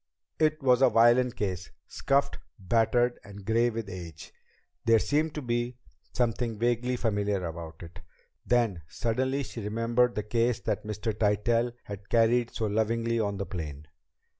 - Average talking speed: Yes, average, 150 wpm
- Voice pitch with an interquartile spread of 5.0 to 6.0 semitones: No, average, 3.0 semitones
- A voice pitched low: Yes, low, 115 Hz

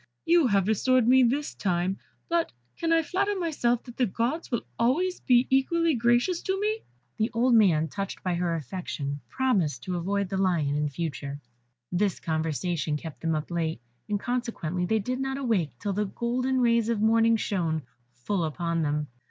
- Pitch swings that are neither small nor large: No, wide, 7.2 semitones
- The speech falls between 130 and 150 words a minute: No, average, 185 wpm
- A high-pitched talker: Yes, high, 210 Hz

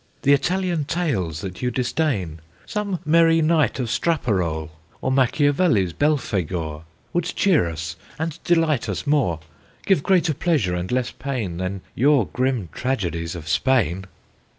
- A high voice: No, low, 130 Hz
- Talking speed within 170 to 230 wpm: No, slow, 135 wpm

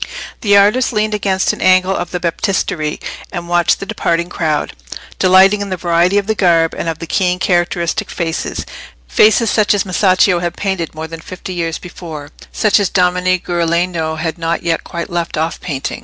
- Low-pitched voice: No, medium, 175 Hz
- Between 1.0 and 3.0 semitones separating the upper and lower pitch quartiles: Yes, narrow, 2.5 semitones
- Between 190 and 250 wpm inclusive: No, average, 180 wpm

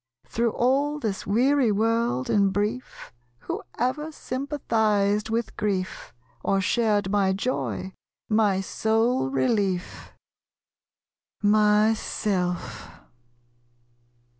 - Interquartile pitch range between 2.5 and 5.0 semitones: Yes, average, 3.4 semitones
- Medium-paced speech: No, slow, 85 wpm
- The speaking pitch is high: Yes, high, 210 Hz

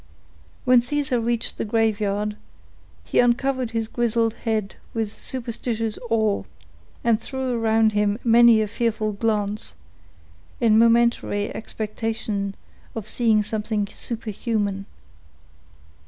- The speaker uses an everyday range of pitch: No, narrow, 2.0 semitones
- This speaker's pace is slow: Yes, slow, 105 wpm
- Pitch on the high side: Yes, high, 225 Hz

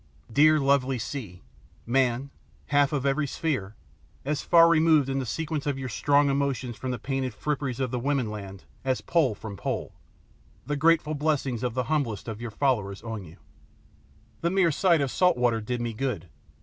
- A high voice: No, low, 135 Hz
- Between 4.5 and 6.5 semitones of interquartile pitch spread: No, average, 3.8 semitones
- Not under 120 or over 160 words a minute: No, average, 180 wpm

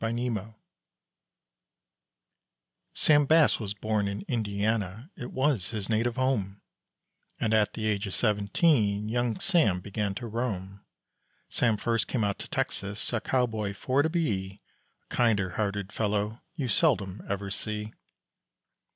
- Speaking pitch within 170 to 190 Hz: No, low, 110 Hz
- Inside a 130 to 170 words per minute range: Yes, slow, 135 wpm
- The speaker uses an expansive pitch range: No, average, 3.2 semitones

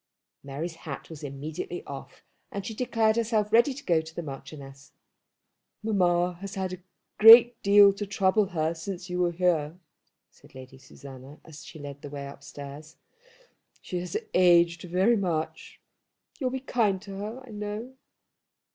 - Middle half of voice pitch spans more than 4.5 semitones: Yes, average, 5.1 semitones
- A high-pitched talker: No, medium, 180 Hz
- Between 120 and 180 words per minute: Yes, average, 155 wpm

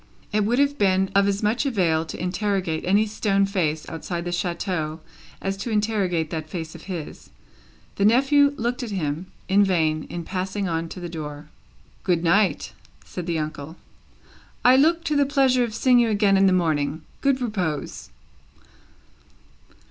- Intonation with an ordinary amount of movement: Yes, average, 4.8 semitones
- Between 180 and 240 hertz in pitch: Yes, high, 190 Hz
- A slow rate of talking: No, average, 165 wpm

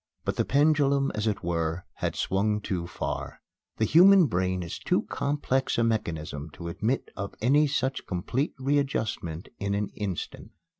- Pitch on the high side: No, low, 105 Hz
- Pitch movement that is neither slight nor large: No, wide, 7.6 semitones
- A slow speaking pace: No, average, 155 wpm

